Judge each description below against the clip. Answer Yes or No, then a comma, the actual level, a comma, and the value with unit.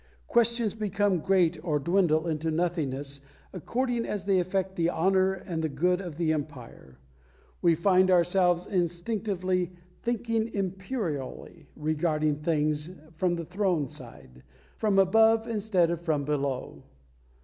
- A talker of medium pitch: Yes, medium, 175 Hz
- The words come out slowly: Yes, slow, 125 wpm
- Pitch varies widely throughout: No, average, 3.8 semitones